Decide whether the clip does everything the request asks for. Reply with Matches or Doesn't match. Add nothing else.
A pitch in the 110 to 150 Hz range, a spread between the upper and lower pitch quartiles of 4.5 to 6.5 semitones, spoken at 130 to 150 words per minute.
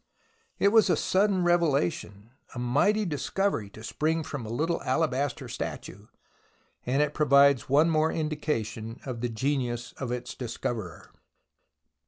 Matches